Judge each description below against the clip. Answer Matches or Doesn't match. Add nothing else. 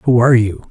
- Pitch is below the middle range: Matches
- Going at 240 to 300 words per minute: Matches